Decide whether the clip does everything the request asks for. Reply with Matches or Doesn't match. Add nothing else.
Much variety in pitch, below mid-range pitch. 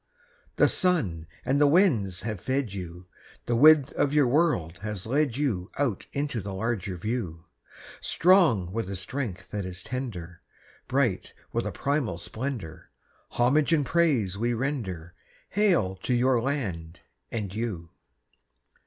Matches